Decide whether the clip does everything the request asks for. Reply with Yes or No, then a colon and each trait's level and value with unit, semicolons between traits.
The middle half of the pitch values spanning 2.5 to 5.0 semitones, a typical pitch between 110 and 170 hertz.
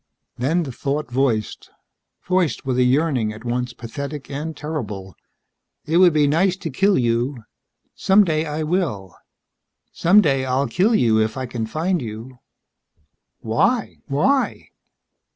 No: wide, 5.4 semitones; medium, 140 Hz